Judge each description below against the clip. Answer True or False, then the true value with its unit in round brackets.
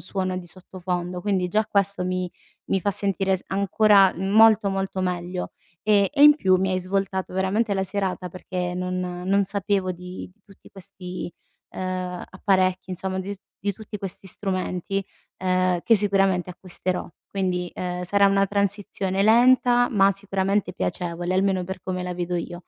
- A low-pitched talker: False (190 Hz)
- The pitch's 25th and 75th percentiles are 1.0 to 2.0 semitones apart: True (1.5 semitones)